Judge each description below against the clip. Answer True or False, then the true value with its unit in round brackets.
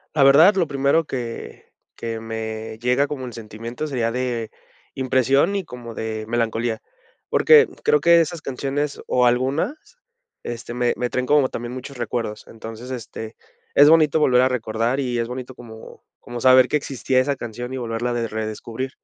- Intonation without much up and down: False (3.1 semitones)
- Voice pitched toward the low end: True (125 Hz)